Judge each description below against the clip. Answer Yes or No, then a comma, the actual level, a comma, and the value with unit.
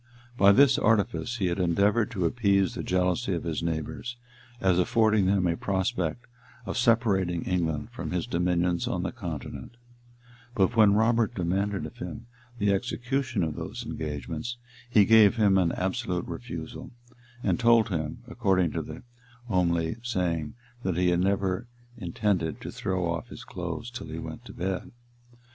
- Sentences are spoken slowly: No, average, 155 wpm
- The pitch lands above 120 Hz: No, very low, 95 Hz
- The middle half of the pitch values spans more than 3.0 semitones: Yes, average, 4.5 semitones